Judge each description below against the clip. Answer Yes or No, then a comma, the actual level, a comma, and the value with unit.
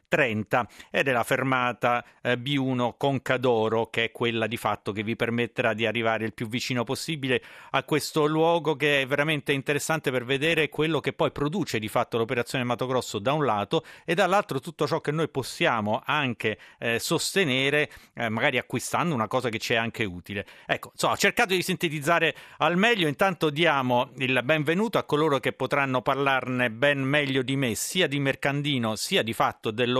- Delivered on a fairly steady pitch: No, average, 4.0 semitones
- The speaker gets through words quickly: Yes, fast, 180 wpm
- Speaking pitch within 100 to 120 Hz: No, low, 135 Hz